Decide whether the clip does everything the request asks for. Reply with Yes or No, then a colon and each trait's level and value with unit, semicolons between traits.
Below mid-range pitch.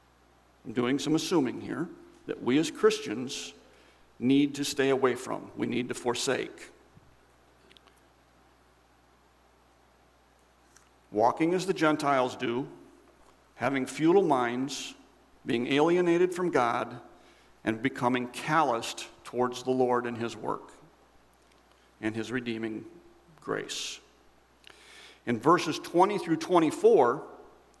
Yes: low, 130 Hz